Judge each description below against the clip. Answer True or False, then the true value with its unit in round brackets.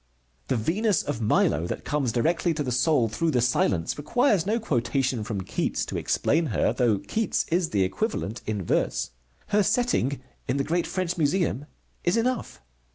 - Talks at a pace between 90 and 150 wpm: False (170 wpm)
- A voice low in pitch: False (145 Hz)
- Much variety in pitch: True (7.5 semitones)